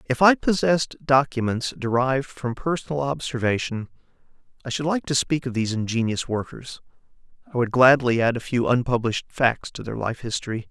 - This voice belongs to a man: Yes, male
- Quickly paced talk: No, average, 160 wpm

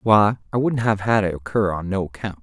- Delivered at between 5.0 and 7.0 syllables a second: Yes, 5.4 syllables/s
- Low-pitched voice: Yes, low, 100 Hz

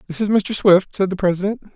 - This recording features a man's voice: Yes, male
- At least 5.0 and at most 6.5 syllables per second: Yes, 6.0 syllables/s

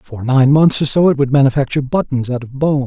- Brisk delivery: Yes, fast, 250 wpm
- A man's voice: Yes, male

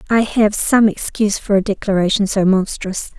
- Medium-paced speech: Yes, average, 170 wpm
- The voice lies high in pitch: Yes, high, 205 Hz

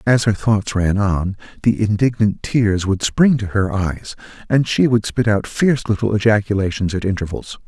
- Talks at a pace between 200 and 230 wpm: No, average, 180 wpm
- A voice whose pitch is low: Yes, low, 105 Hz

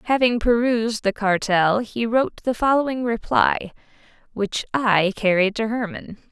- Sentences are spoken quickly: No, slow, 135 wpm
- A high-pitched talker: Yes, high, 220 Hz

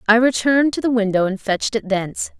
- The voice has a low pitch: No, high, 220 Hz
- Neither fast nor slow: No, fast, 225 wpm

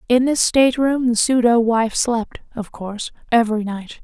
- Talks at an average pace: Yes, average, 180 wpm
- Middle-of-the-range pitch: No, high, 235 Hz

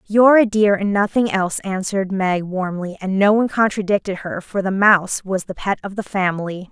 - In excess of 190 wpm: Yes, fast, 205 wpm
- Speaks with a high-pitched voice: Yes, high, 195 Hz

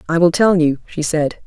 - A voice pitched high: No, medium, 165 Hz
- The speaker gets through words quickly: Yes, fast, 245 wpm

